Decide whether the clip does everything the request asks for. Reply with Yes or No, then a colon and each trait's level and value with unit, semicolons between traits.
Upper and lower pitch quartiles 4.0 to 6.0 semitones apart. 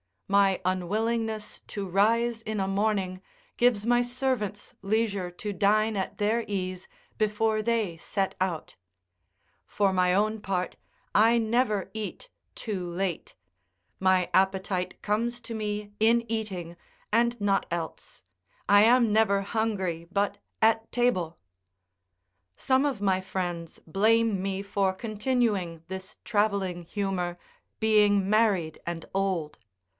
No: average, 2.9 semitones